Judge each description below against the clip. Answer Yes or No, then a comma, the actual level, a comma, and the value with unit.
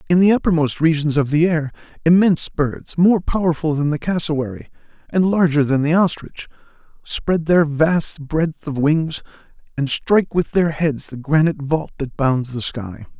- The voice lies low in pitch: No, medium, 155 Hz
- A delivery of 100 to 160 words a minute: No, average, 170 wpm